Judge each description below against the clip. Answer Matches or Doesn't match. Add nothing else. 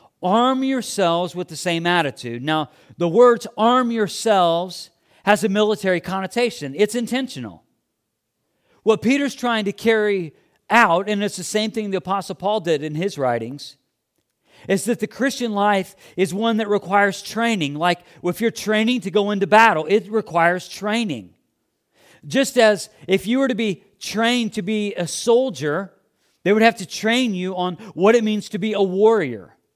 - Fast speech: Doesn't match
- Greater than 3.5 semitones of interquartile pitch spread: Matches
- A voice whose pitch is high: Matches